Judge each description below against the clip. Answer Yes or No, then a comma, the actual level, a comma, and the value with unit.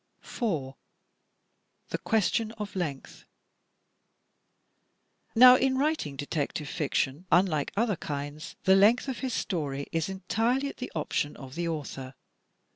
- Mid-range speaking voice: Yes, medium, 175 Hz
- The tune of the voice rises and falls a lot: Yes, wide, 7.8 semitones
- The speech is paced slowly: Yes, slow, 120 wpm